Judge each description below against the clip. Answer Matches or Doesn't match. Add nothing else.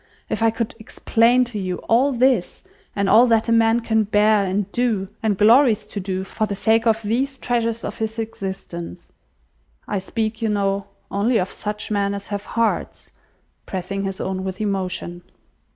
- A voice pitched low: Doesn't match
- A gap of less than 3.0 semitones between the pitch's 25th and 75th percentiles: Matches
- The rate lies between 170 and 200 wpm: Matches